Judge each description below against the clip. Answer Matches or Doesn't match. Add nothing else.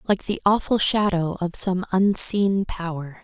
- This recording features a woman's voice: Matches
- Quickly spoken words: Doesn't match